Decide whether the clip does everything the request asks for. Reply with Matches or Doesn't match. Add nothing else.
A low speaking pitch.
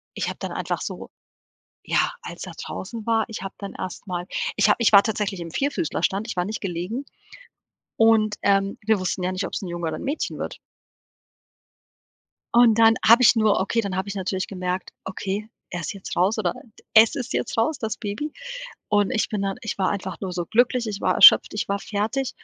Doesn't match